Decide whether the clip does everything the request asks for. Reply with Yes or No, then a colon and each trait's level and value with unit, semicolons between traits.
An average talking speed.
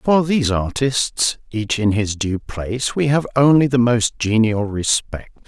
Yes: average, 165 wpm